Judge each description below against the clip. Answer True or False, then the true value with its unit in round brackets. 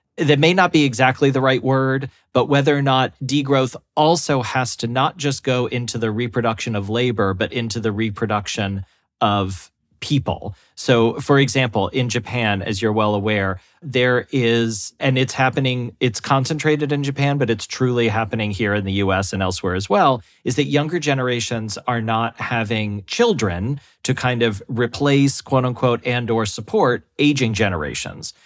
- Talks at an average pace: True (165 wpm)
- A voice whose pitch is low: True (120 Hz)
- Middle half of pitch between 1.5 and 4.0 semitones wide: True (3.7 semitones)